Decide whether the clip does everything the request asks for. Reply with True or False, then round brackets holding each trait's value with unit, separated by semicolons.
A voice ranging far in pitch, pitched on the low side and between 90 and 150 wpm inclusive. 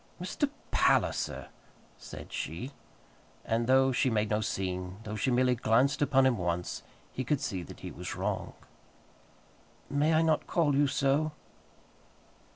False (4.9 semitones; 130 Hz; 145 wpm)